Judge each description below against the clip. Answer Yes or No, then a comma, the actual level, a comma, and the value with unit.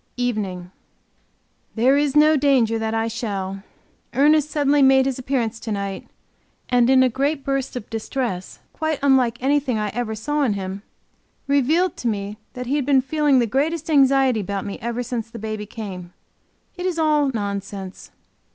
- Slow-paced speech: No, average, 170 wpm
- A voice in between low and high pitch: No, high, 245 Hz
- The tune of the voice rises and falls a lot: No, average, 4.6 semitones